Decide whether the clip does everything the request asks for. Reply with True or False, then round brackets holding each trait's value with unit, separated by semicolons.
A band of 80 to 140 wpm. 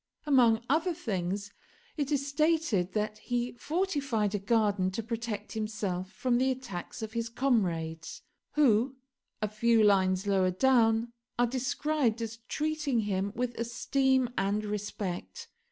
True (135 wpm)